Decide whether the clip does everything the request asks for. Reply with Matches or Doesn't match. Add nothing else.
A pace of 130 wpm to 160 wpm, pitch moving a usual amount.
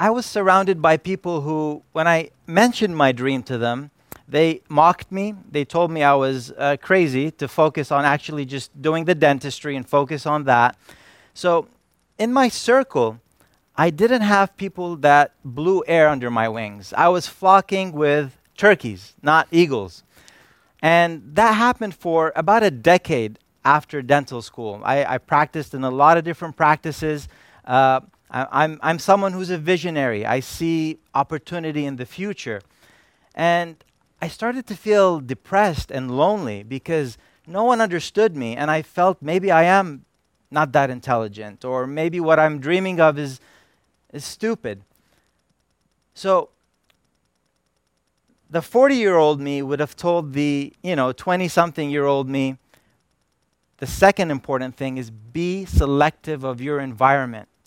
Matches